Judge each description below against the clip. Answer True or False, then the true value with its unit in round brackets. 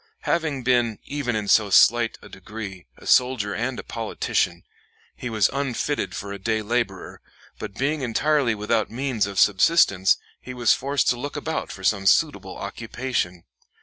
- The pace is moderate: True (160 wpm)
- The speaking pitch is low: True (115 Hz)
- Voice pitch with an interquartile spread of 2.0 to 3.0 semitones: False (4.3 semitones)